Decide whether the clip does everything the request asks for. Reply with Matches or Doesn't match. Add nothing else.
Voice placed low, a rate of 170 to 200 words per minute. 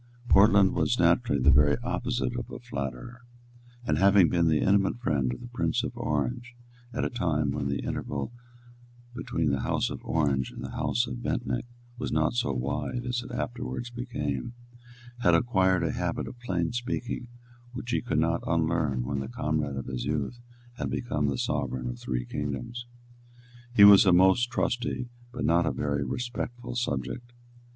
Matches